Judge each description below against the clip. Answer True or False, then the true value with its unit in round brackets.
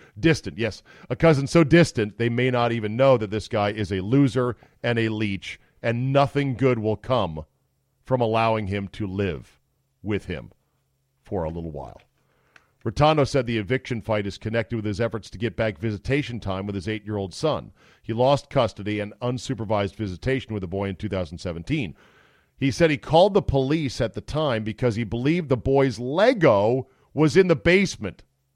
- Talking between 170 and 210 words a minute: True (185 wpm)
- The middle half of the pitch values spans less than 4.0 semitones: False (4.3 semitones)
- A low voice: True (115 Hz)